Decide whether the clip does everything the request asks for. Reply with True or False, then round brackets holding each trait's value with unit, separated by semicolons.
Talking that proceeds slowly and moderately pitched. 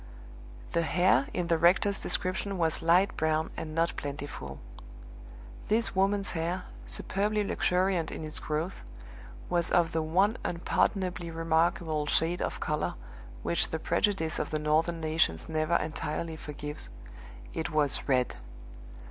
True (130 wpm; 165 Hz)